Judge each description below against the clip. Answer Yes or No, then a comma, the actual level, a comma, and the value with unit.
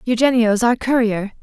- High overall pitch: Yes, high, 230 Hz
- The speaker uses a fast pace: No, slow, 125 wpm